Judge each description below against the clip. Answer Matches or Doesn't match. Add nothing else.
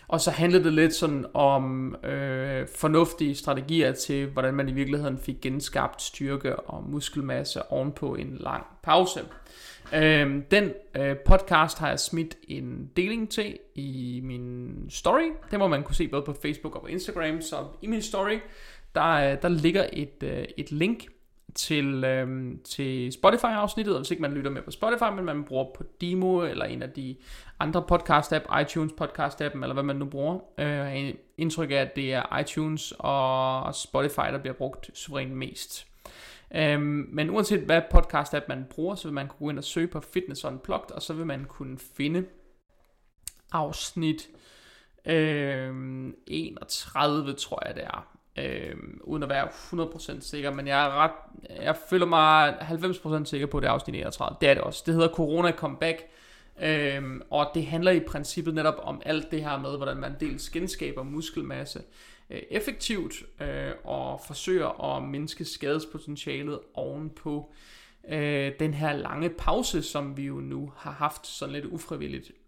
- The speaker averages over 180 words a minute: Doesn't match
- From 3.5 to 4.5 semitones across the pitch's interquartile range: Doesn't match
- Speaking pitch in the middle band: Matches